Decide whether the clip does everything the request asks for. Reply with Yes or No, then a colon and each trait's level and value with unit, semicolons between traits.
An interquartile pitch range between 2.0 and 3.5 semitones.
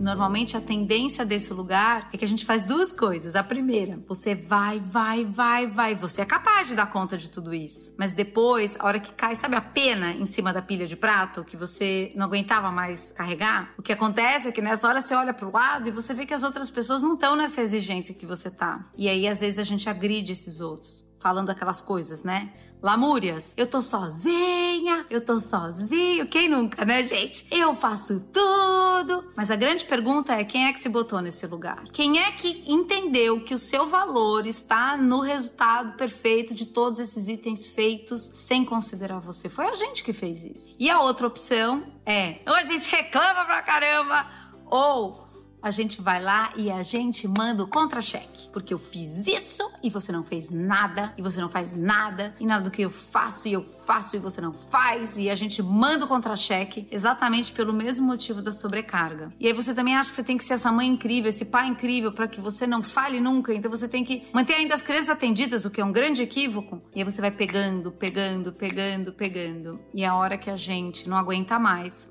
No: average, 4.5 semitones